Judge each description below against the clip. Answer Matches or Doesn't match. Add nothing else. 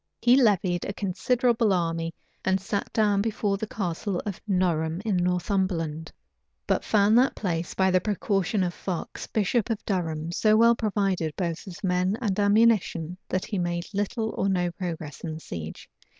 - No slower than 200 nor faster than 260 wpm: Doesn't match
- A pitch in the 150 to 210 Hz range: Matches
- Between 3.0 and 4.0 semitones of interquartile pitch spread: Matches